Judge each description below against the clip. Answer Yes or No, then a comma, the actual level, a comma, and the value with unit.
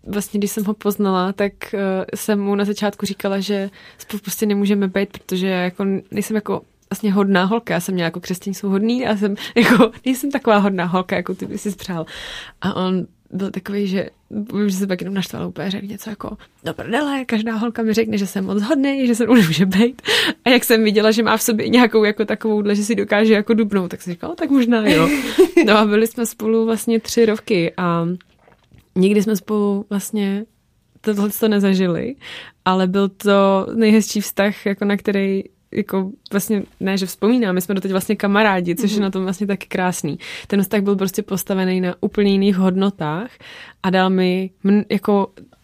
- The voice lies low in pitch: No, high, 205 Hz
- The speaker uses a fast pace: Yes, fast, 195 wpm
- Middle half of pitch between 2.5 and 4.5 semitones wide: No, narrow, 2.1 semitones